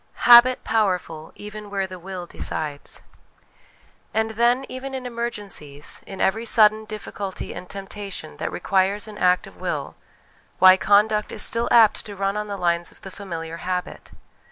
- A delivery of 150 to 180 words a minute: Yes, average, 155 wpm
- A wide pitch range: No, average, 3.0 semitones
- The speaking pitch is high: Yes, high, 200 Hz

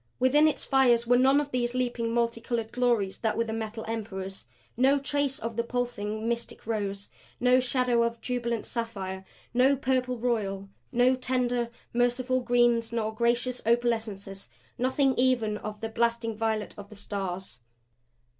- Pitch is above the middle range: Yes, high, 235 Hz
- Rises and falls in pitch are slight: Yes, narrow, 2.3 semitones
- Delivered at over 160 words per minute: No, average, 150 wpm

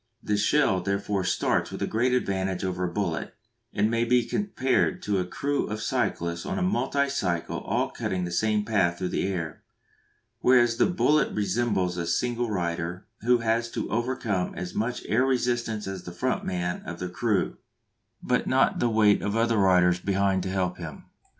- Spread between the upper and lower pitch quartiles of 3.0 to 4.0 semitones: No, average, 4.7 semitones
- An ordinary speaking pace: Yes, average, 180 wpm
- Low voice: Yes, low, 100 Hz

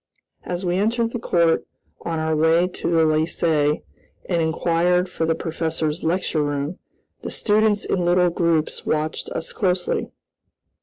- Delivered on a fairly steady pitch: Yes, narrow, 2.1 semitones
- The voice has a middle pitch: Yes, medium, 170 Hz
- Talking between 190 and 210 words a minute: No, average, 145 wpm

